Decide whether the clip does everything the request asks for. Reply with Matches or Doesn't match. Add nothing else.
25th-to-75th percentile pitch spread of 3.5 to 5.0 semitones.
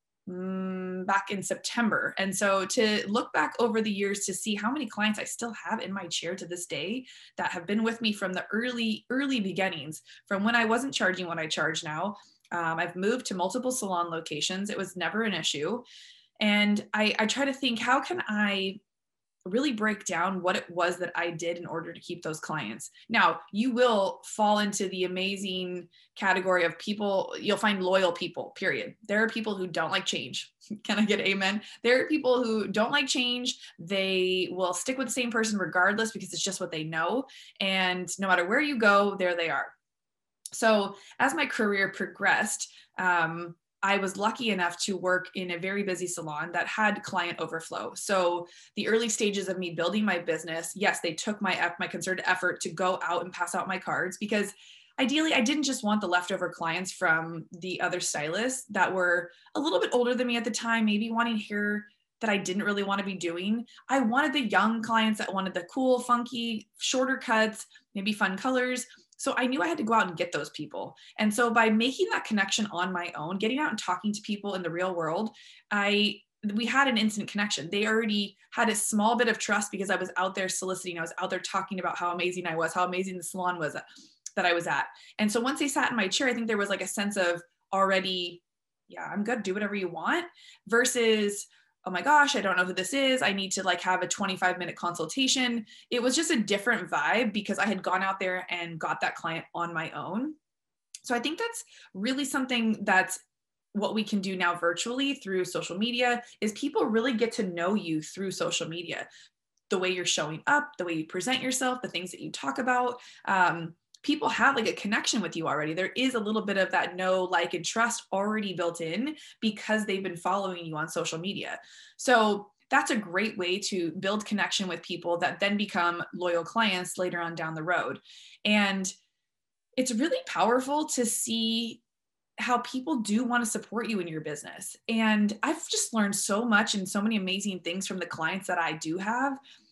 Matches